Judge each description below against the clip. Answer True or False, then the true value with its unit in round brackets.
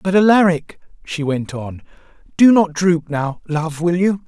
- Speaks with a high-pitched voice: False (170 Hz)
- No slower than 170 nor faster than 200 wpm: False (155 wpm)